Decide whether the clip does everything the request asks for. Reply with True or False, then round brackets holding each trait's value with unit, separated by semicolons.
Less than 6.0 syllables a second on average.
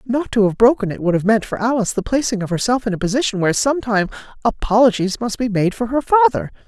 False (6.7 syllables/s)